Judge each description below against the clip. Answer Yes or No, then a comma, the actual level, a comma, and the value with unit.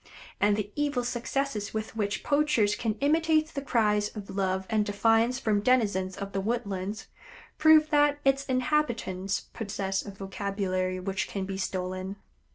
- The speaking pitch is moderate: No, high, 210 Hz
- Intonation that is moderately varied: Yes, average, 4.8 semitones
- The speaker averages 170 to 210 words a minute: No, average, 150 wpm